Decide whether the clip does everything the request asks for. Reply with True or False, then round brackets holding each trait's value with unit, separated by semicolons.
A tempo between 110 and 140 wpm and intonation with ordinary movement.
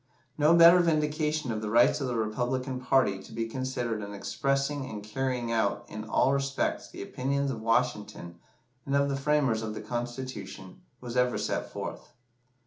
False (170 wpm; 3.7 semitones)